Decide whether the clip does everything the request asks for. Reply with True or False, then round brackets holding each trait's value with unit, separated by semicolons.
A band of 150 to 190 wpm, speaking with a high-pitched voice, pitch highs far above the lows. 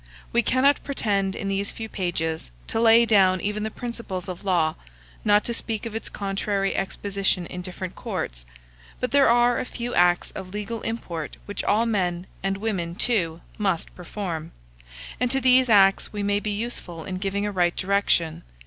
False (175 wpm; 200 Hz; 3.8 semitones)